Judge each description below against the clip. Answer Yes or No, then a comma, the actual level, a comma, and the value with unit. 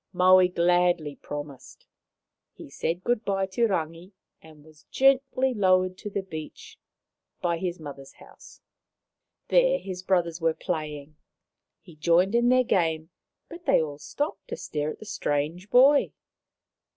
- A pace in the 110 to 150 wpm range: Yes, average, 140 wpm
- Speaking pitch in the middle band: Yes, medium, 180 Hz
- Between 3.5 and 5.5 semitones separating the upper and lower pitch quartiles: Yes, average, 4.8 semitones